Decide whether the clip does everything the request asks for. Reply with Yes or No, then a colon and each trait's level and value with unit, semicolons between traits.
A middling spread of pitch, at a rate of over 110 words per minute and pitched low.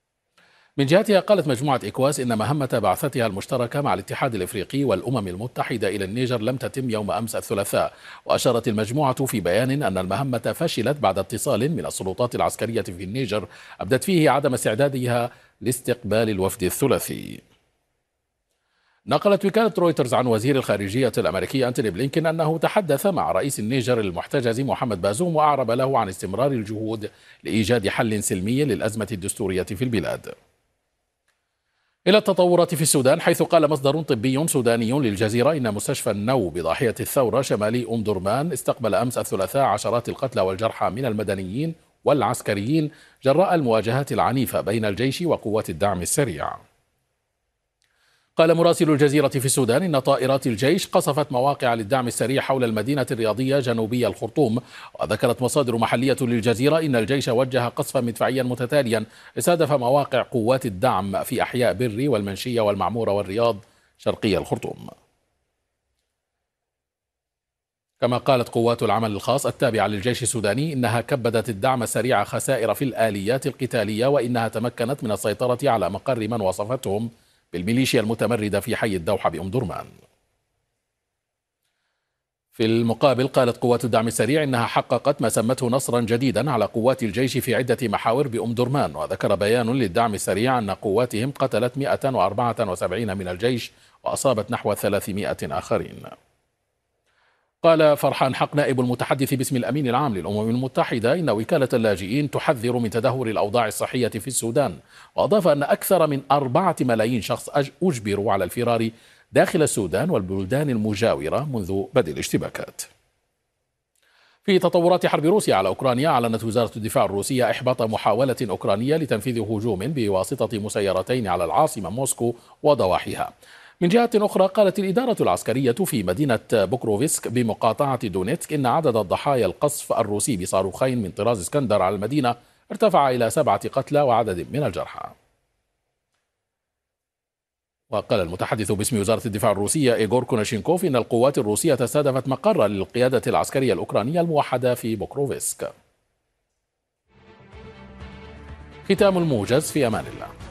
Yes: average, 4.1 semitones; average, 130 wpm; low, 125 Hz